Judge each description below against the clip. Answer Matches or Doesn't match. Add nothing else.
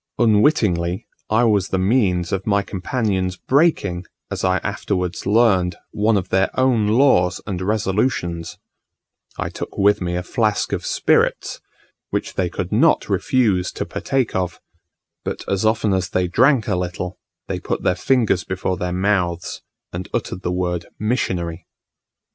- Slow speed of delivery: Doesn't match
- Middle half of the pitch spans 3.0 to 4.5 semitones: Matches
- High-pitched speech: Doesn't match